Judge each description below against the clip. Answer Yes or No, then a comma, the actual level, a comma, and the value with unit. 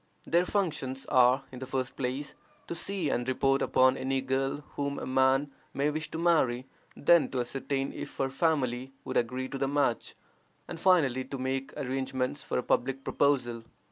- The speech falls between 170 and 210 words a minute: Yes, average, 175 wpm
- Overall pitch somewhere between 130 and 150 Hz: Yes, low, 135 Hz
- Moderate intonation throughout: No, narrow, 1.8 semitones